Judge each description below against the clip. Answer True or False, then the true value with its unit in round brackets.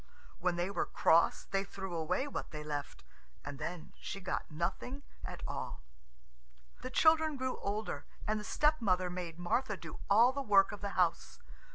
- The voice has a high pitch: True (195 Hz)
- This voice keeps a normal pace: True (170 wpm)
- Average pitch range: False (6.0 semitones)